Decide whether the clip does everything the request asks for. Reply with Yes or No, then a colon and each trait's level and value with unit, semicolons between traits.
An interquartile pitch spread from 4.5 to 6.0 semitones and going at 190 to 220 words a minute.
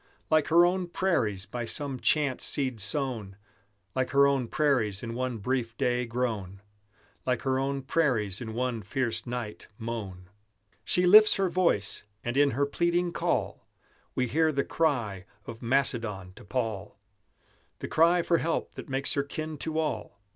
No: average, 5.1 semitones; average, 160 wpm